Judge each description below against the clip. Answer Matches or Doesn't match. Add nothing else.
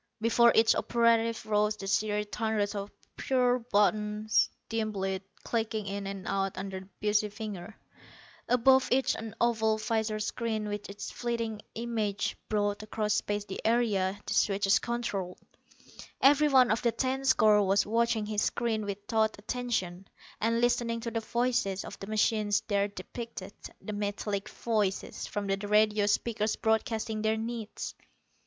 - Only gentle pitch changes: Matches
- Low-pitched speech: Doesn't match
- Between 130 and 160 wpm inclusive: Matches